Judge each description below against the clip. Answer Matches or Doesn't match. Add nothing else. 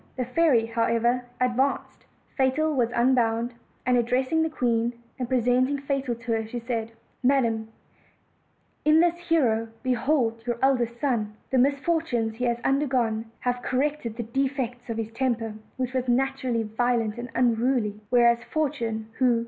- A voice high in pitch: Matches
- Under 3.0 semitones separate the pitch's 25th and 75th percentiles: Matches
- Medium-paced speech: Matches